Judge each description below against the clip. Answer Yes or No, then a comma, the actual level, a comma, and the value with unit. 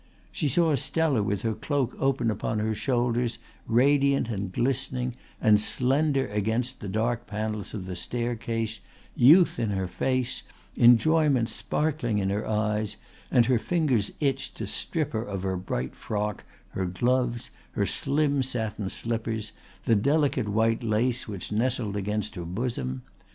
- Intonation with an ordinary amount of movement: Yes, average, 3.7 semitones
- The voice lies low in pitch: Yes, low, 115 Hz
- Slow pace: No, average, 145 wpm